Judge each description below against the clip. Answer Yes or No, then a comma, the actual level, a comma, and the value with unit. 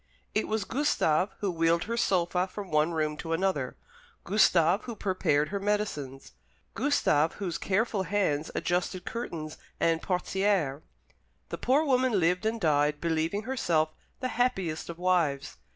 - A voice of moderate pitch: Yes, medium, 180 Hz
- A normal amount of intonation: Yes, average, 4.6 semitones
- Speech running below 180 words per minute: Yes, average, 140 wpm